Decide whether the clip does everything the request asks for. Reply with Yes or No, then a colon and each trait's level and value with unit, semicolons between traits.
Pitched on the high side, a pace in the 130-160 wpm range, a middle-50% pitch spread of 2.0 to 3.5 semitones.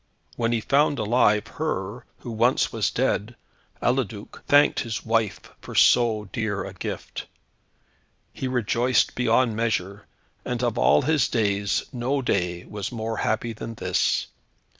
No: low, 115 Hz; average, 140 wpm; average, 2.9 semitones